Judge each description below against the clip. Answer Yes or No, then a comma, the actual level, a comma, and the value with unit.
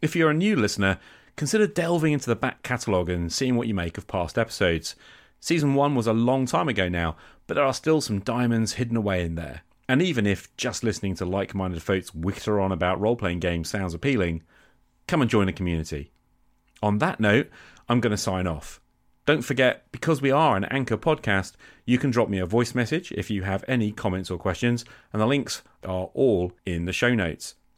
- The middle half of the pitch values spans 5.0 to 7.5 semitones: Yes, wide, 5.4 semitones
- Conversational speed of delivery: No, fast, 210 wpm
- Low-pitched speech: Yes, low, 105 Hz